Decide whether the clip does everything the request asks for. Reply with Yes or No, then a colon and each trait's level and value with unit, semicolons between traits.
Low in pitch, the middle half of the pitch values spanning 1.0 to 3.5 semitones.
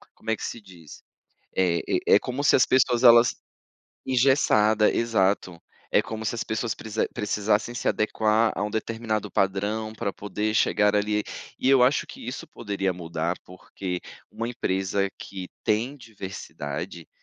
Yes: low, 105 Hz; average, 3.1 semitones